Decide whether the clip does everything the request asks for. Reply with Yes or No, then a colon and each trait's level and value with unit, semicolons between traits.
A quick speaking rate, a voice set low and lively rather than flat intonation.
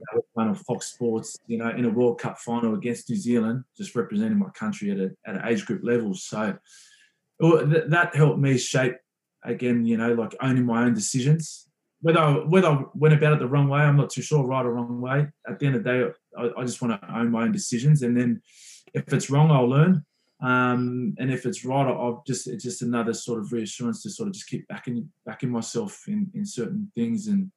Yes: fast, 230 wpm; low, 130 Hz; wide, 5.7 semitones